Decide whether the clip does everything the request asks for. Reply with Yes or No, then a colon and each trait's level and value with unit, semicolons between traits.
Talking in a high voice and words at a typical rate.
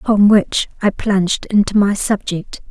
Yes: high, 200 Hz; average, 155 wpm